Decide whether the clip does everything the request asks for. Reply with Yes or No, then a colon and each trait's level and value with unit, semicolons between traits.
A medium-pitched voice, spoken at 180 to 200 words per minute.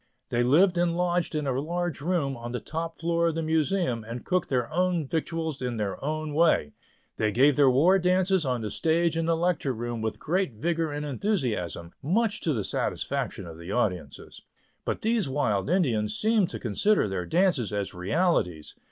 Yes: medium, 150 Hz; average, 185 wpm